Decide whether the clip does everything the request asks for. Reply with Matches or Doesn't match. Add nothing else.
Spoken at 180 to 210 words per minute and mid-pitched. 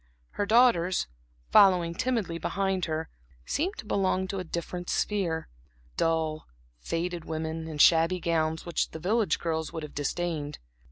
Doesn't match